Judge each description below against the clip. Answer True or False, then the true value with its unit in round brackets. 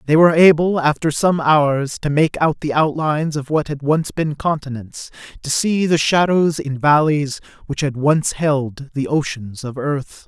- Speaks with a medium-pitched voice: True (150 Hz)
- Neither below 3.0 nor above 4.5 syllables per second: True (4.3 syllables/s)